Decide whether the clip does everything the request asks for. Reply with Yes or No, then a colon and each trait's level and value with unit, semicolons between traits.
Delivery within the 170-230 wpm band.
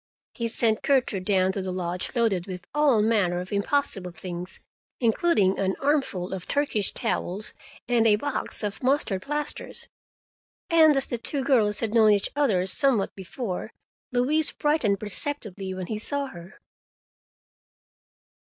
No: average, 140 wpm